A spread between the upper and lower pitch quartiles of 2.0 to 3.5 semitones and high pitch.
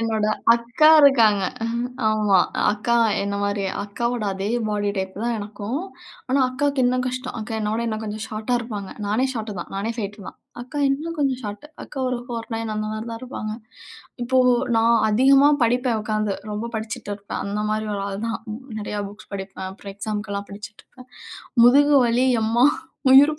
Yes: average, 3.2 semitones; high, 220 Hz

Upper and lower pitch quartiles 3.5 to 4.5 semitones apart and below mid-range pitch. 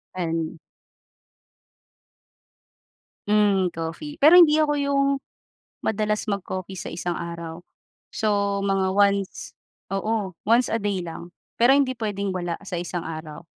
No: average, 4.1 semitones; high, 195 Hz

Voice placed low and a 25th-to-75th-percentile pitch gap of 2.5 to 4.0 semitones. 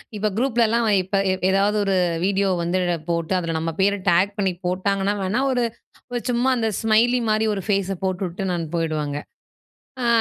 No: high, 195 Hz; average, 3.3 semitones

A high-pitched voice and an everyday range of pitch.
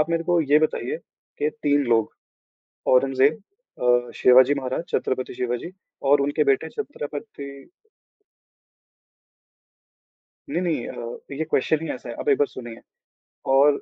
No: medium, 140 Hz; average, 3.1 semitones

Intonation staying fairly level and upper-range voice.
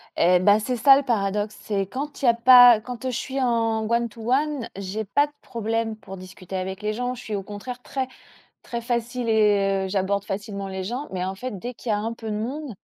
No: average, 3.8 semitones; high, 225 Hz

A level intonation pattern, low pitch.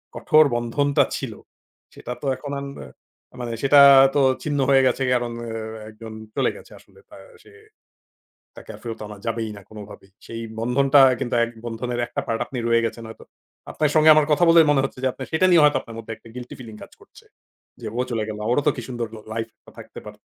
No: average, 3.6 semitones; low, 120 Hz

